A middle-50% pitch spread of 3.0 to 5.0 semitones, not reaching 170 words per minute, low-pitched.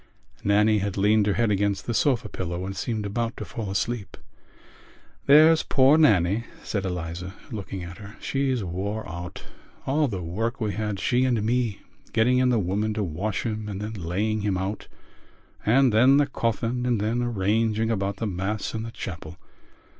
No: average, 3.3 semitones; average, 175 wpm; low, 105 Hz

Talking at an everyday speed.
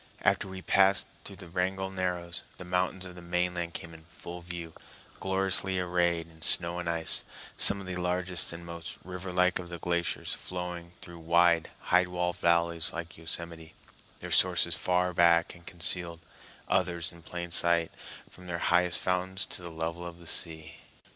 Yes: average, 175 wpm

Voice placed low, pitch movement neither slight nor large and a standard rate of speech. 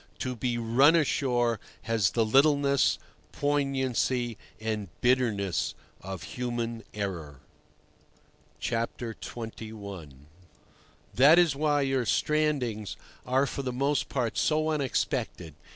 No: low, 125 Hz; average, 3.8 semitones; slow, 100 wpm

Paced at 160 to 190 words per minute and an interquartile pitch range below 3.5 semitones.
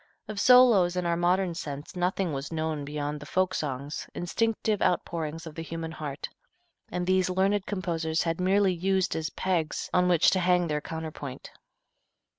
Yes: average, 165 wpm; average, 3.0 semitones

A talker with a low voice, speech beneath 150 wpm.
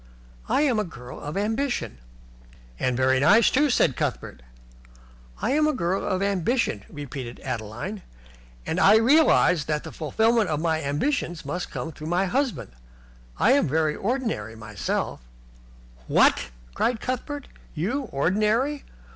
No: medium, 180 Hz; average, 140 wpm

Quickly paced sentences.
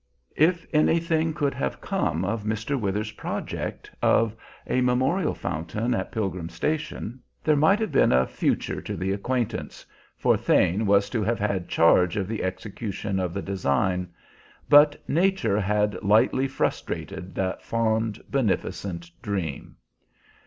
No: average, 140 wpm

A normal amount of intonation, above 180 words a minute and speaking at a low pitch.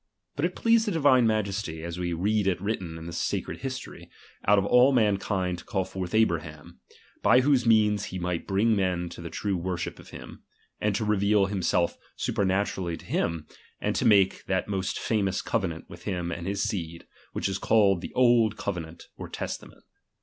Yes: average, 3.7 semitones; average, 195 wpm; very low, 95 Hz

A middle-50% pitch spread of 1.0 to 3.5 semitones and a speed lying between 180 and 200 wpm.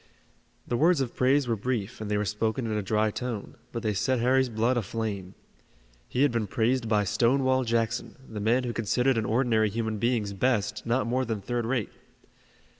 Yes: average, 2.8 semitones; average, 190 wpm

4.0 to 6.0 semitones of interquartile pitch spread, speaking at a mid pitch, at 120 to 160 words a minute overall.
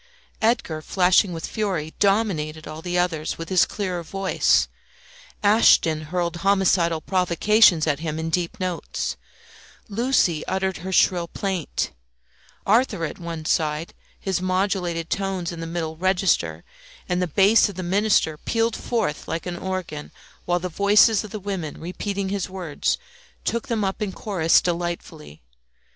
No: average, 3.1 semitones; medium, 180 Hz; average, 145 wpm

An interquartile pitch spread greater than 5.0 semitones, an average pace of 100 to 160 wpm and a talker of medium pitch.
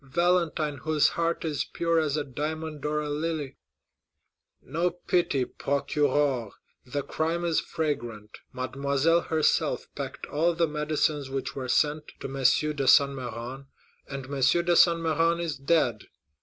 No: average, 3.2 semitones; average, 145 wpm; medium, 150 Hz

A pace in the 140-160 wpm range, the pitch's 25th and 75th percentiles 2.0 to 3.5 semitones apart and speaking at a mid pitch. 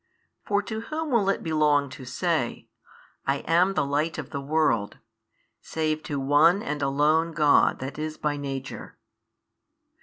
Yes: average, 150 wpm; average, 2.8 semitones; medium, 150 Hz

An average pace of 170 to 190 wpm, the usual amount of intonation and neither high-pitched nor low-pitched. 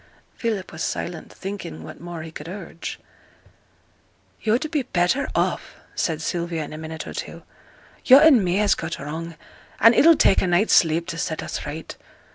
Yes: average, 175 wpm; average, 4.2 semitones; medium, 175 Hz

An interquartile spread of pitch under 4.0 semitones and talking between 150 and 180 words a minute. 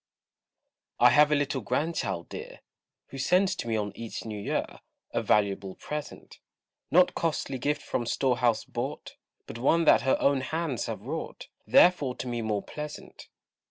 No: average, 5.0 semitones; average, 160 wpm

